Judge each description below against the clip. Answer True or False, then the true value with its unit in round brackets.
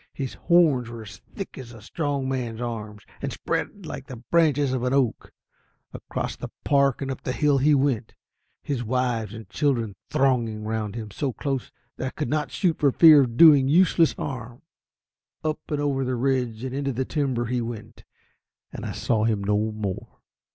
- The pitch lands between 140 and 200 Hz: False (130 Hz)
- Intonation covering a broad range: False (3.7 semitones)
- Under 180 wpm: False (185 wpm)